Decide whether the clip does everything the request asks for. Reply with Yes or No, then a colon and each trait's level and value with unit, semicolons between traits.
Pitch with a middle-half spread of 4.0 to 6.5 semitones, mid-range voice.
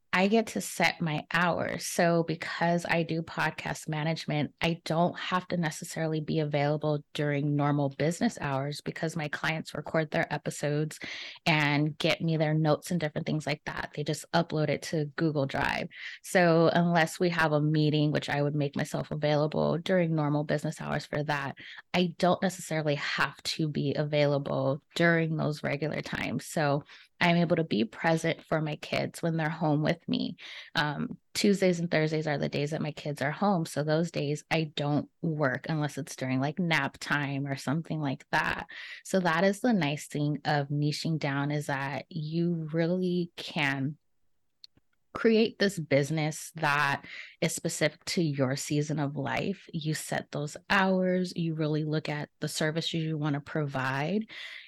No: narrow, 2.5 semitones; medium, 155 Hz